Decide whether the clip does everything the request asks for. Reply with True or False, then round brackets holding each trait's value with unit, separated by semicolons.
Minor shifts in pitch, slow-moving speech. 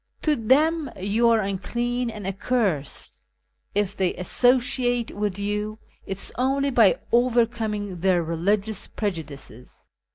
False (4.0 semitones; 120 wpm)